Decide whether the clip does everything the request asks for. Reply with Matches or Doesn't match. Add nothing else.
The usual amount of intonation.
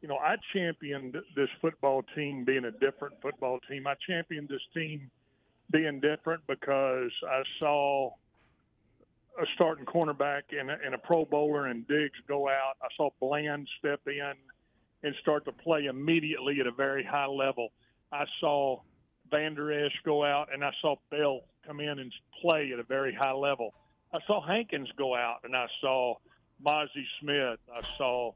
Doesn't match